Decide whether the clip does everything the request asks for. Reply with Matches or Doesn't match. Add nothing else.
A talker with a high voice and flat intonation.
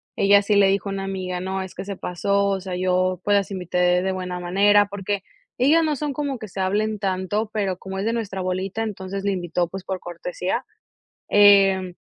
Matches